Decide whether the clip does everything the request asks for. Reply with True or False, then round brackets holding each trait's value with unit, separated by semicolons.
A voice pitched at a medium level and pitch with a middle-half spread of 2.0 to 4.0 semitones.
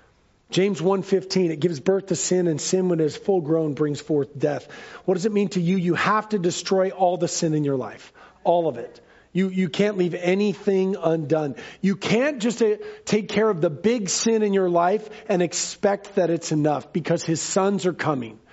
True (180 Hz; 3.7 semitones)